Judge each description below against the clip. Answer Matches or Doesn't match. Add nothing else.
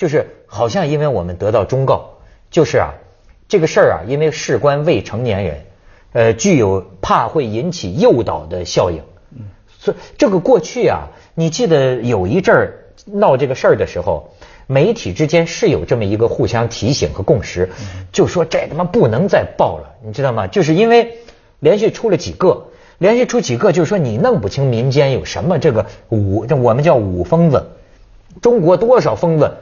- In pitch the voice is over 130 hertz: Matches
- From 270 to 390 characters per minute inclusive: Matches